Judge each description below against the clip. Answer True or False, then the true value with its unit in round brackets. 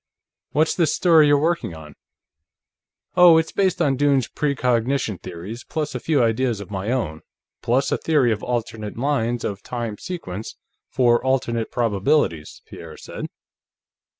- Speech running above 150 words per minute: False (145 wpm)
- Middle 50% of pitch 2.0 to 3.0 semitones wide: False (5.1 semitones)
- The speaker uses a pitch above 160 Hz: False (125 Hz)